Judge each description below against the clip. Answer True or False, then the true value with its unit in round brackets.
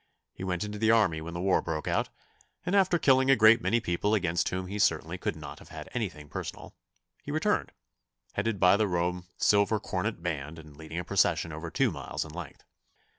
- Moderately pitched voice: False (90 Hz)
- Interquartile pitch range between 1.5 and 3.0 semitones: False (4.4 semitones)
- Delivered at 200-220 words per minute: True (205 wpm)